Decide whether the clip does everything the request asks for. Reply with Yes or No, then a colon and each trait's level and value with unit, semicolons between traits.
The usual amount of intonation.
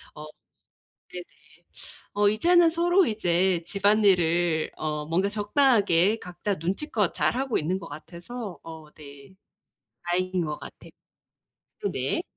Yes: average, 4.4 semitones